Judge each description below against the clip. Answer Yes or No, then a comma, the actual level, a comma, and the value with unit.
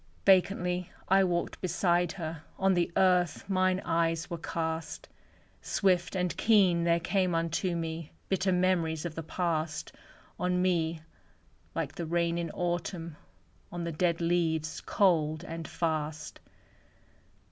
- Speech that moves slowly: Yes, slow, 130 wpm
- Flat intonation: Yes, narrow, 1.8 semitones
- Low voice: No, medium, 170 Hz